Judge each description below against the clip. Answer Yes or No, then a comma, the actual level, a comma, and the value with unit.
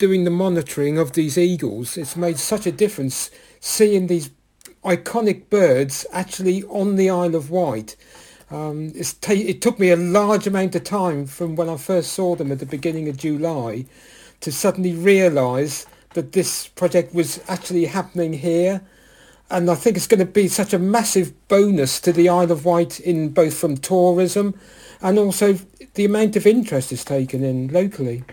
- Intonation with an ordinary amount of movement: Yes, average, 3.3 semitones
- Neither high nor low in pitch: Yes, medium, 175 Hz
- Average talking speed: Yes, average, 170 wpm